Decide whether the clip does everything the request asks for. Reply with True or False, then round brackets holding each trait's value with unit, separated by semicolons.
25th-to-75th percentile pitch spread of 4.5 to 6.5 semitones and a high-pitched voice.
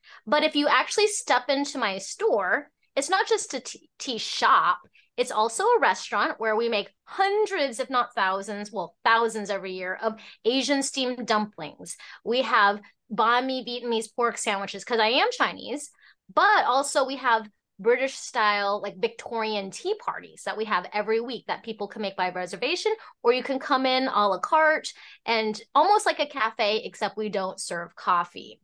True (5.1 semitones; 230 Hz)